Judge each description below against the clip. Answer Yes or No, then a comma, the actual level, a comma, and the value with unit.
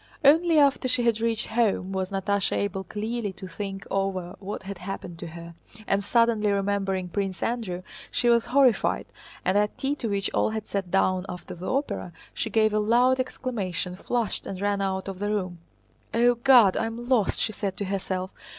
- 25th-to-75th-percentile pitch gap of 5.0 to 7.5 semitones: No, average, 3.6 semitones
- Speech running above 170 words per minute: Yes, average, 190 wpm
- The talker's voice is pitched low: No, high, 200 Hz